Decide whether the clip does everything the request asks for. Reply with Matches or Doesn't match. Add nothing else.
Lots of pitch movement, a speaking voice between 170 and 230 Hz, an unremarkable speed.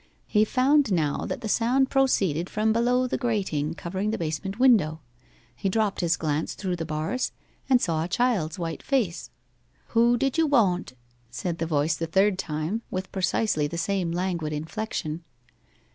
Matches